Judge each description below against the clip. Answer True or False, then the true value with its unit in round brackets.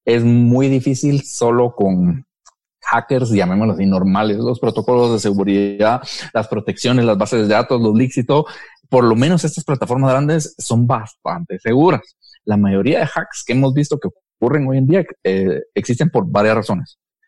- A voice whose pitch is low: True (120 Hz)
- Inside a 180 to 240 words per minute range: False (170 wpm)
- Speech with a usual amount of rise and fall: True (4.2 semitones)